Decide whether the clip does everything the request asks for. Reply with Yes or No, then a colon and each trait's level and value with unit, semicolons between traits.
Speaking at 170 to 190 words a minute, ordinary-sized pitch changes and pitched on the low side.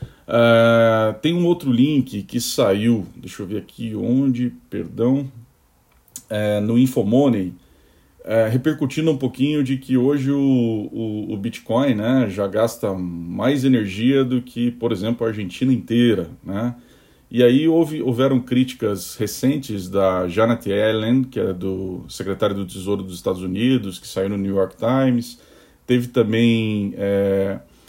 No: average, 145 wpm; average, 4.4 semitones; low, 115 Hz